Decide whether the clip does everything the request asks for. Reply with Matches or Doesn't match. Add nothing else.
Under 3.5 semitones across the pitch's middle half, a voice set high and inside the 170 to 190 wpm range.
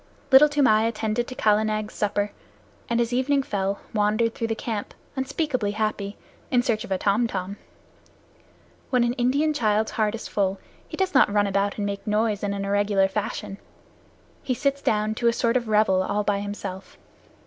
Matches